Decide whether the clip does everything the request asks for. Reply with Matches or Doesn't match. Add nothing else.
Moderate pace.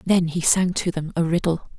Doesn't match